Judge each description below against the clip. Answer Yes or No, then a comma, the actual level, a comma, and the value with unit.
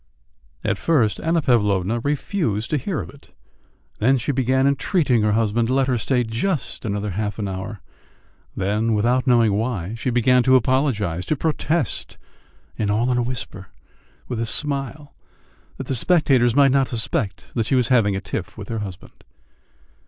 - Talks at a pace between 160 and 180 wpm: Yes, average, 165 wpm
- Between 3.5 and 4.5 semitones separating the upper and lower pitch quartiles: Yes, average, 4.2 semitones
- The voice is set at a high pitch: No, low, 120 Hz